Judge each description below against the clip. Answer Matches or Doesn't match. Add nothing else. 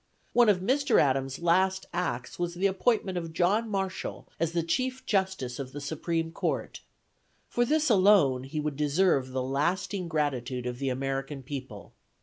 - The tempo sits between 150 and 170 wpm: Matches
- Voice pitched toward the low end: Doesn't match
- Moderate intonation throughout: Doesn't match